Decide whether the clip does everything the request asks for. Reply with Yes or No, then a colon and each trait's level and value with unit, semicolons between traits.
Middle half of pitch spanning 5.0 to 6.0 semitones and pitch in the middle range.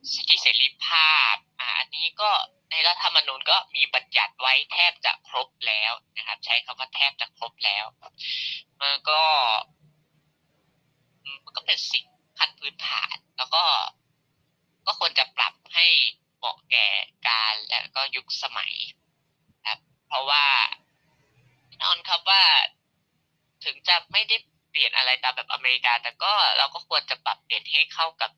No: average, 4.4 semitones; medium, 150 Hz